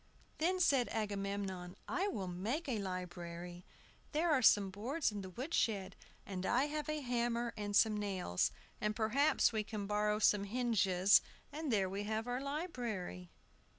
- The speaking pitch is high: Yes, high, 210 Hz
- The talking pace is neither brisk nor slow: Yes, average, 160 wpm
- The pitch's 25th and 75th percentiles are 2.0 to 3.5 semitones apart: No, average, 4.6 semitones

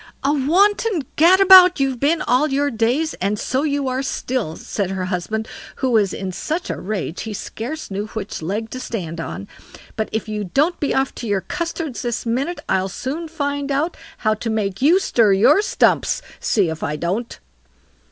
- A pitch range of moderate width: No, wide, 6.5 semitones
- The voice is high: Yes, high, 245 Hz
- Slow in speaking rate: No, average, 185 wpm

